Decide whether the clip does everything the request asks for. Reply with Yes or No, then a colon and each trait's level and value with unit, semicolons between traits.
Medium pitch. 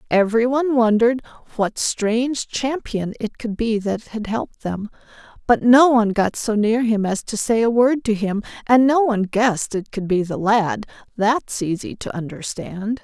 No: high, 220 Hz